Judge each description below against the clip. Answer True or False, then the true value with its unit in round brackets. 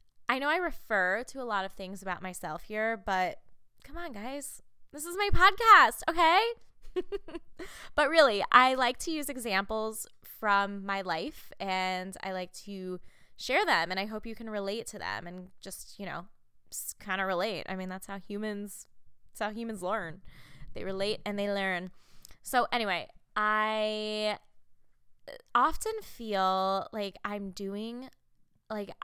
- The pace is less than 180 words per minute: True (155 wpm)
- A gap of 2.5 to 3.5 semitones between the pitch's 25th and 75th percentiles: False (4.6 semitones)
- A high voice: True (205 Hz)